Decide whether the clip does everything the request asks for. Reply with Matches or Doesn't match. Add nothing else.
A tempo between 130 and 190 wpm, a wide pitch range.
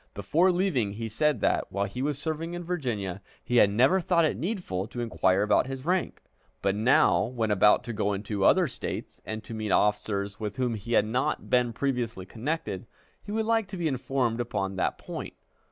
Doesn't match